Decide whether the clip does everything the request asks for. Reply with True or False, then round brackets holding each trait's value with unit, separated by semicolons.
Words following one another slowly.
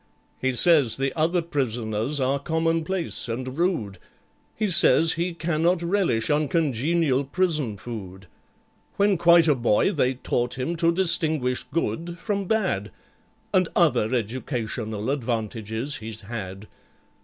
True (120 wpm)